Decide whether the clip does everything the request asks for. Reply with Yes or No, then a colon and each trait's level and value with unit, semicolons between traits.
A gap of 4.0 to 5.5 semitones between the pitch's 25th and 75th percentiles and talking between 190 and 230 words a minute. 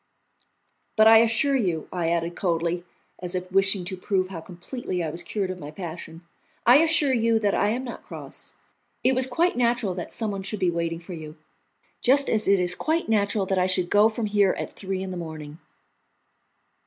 Yes: average, 4.3 semitones; average, 200 wpm